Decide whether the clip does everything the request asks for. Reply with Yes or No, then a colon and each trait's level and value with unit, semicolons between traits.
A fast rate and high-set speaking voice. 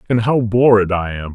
No: fast, 225 wpm; low, 105 Hz